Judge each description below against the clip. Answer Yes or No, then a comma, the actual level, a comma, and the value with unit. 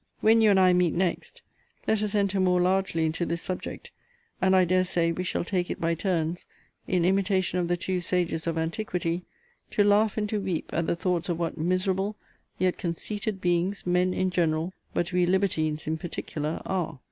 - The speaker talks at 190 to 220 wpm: Yes, average, 195 wpm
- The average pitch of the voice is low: No, medium, 180 Hz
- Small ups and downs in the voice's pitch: Yes, narrow, 2.1 semitones